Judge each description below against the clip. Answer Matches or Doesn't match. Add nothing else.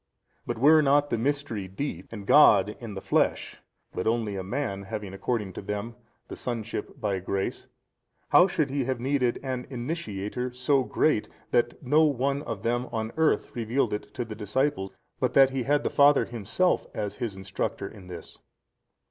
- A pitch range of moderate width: Matches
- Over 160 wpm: Matches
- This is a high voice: Doesn't match